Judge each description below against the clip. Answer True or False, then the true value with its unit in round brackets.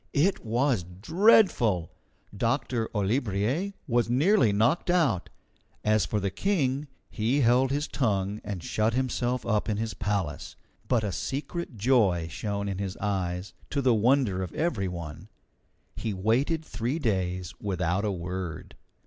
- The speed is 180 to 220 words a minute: False (140 wpm)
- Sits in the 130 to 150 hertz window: False (110 Hz)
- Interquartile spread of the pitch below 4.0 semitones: False (5.3 semitones)